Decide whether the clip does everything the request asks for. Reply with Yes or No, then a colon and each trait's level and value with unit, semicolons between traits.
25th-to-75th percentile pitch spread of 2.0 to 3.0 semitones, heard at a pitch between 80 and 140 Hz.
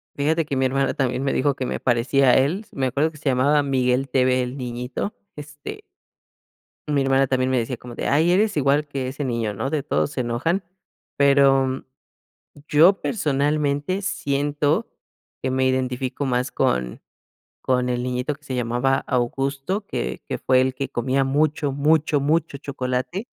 Yes: narrow, 2.4 semitones; low, 135 Hz